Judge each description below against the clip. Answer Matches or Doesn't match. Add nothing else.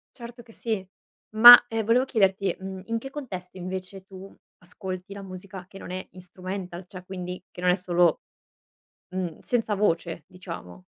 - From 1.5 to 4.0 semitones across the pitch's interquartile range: Matches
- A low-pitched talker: Doesn't match